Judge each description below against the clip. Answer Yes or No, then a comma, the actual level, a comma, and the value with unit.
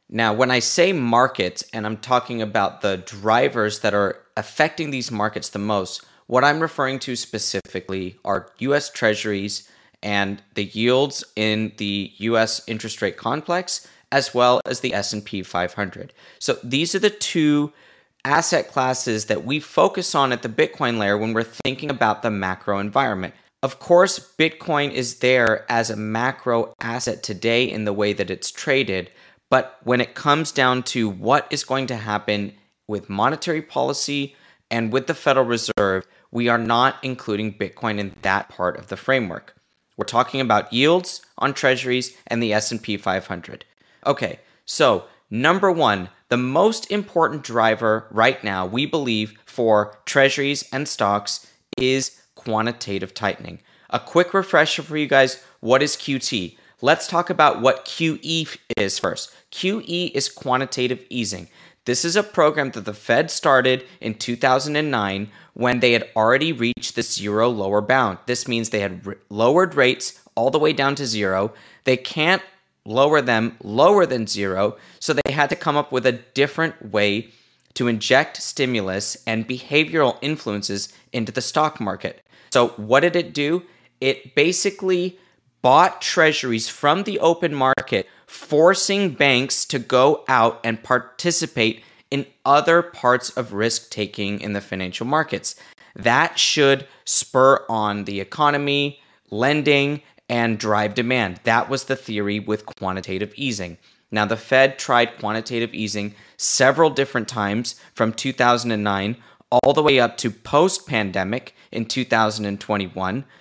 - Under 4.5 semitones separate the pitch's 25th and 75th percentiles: No, average, 4.8 semitones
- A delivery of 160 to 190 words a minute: No, average, 150 wpm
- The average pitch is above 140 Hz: No, low, 120 Hz